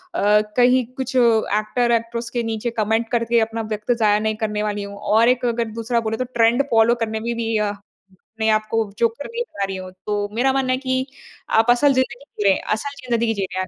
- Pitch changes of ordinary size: No, narrow, 2.2 semitones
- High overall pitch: Yes, high, 230 Hz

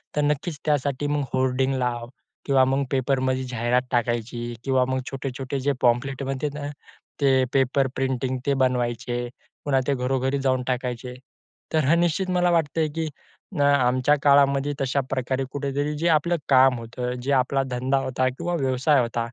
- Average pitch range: No, narrow, 2.1 semitones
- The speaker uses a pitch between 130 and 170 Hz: Yes, low, 135 Hz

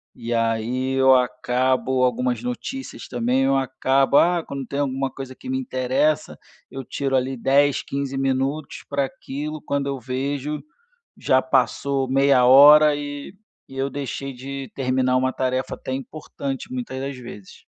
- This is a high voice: No, low, 135 Hz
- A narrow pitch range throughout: Yes, narrow, 1.5 semitones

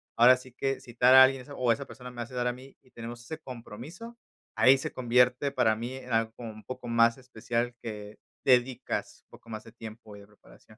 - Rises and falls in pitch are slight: Yes, narrow, 2.0 semitones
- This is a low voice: Yes, low, 125 Hz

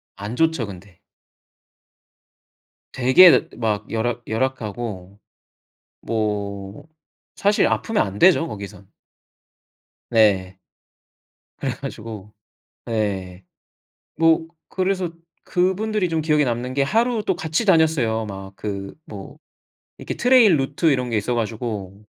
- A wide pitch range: Yes, wide, 7.9 semitones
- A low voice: Yes, low, 120 Hz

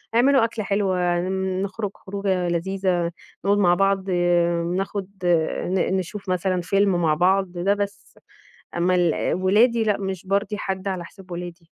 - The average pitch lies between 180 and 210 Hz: Yes, high, 190 Hz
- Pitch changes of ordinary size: No, narrow, 2.1 semitones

